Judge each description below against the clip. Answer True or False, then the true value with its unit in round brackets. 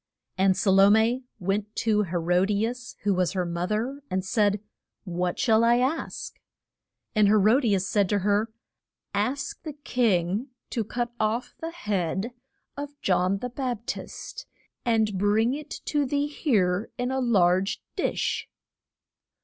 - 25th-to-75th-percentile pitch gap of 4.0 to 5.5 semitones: True (4.3 semitones)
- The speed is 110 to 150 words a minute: False (160 wpm)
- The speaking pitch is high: True (215 Hz)